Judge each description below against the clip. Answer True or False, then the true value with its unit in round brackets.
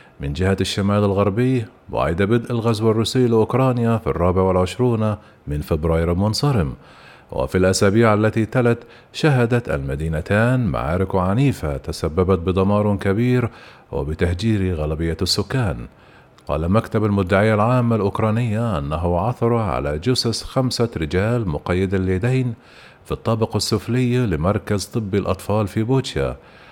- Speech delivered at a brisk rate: False (110 wpm)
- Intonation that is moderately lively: True (4.3 semitones)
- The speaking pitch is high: False (105 Hz)